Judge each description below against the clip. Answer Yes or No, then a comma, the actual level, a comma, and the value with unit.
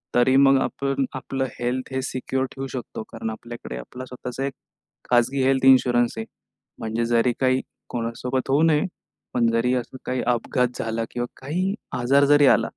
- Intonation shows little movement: Yes, narrow, 2.0 semitones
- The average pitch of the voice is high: No, low, 130 Hz